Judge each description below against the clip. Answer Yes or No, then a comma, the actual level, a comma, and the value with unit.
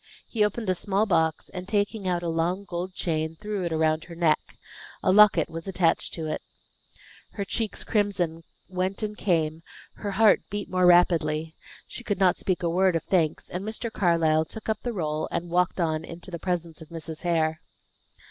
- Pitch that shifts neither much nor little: Yes, average, 3.4 semitones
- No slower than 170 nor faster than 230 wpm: Yes, average, 190 wpm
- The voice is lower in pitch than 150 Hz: No, medium, 175 Hz